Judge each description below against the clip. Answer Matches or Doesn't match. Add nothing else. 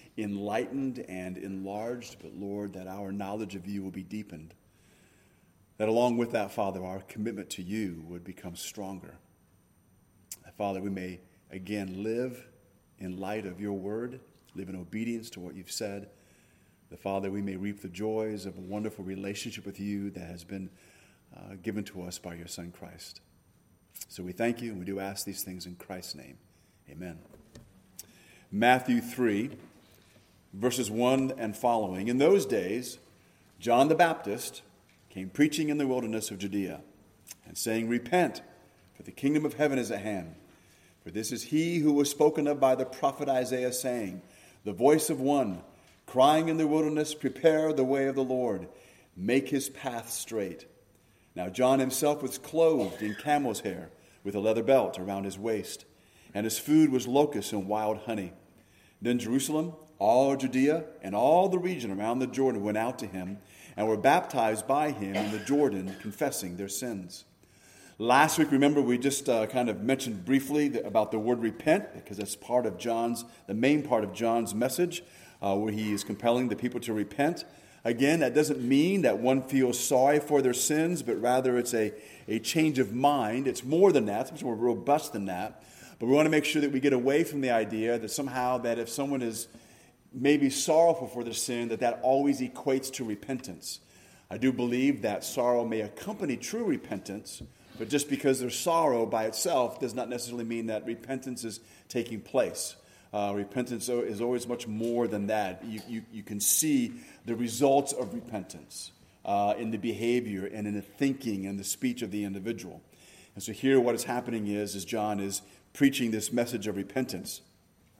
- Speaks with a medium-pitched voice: Doesn't match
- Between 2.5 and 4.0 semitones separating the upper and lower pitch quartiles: Doesn't match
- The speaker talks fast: Doesn't match